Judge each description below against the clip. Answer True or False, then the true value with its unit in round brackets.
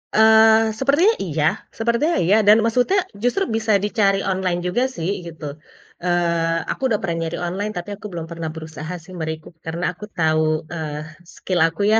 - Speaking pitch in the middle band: True (180 Hz)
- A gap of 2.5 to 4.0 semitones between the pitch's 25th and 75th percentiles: False (5.1 semitones)